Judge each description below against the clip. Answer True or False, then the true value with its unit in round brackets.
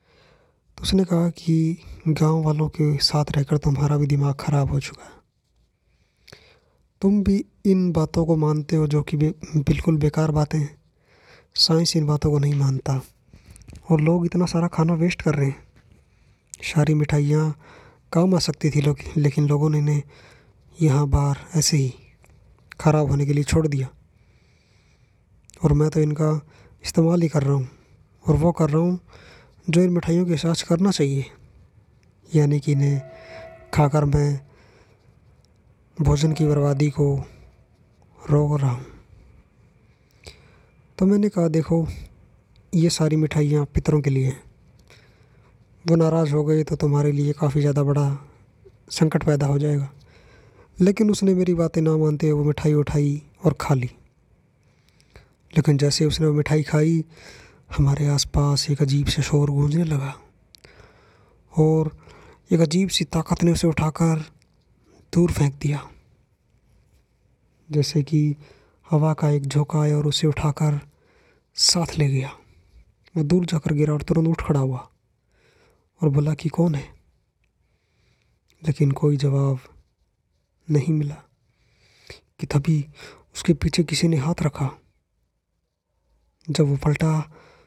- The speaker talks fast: False (140 wpm)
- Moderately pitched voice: True (150 Hz)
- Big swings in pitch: False (2.4 semitones)